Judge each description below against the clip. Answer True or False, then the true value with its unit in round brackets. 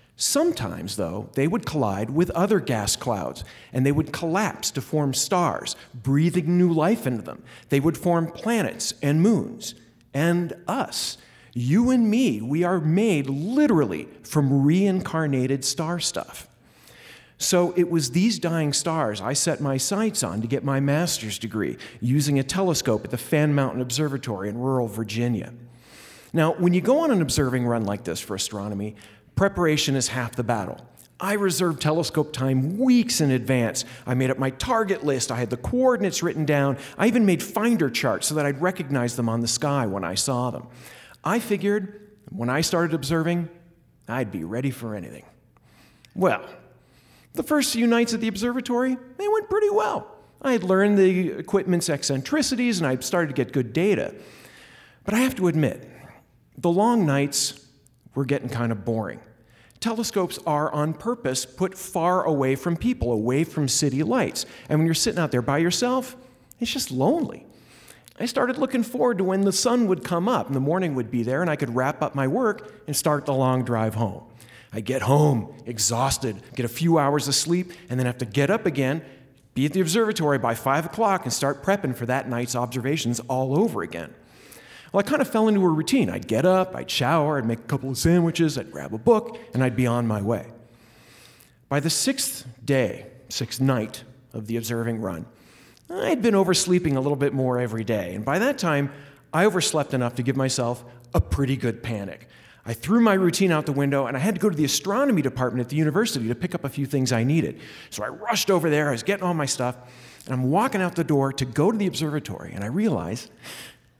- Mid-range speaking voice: True (145 Hz)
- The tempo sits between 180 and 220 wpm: True (195 wpm)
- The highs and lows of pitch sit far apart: True (6.5 semitones)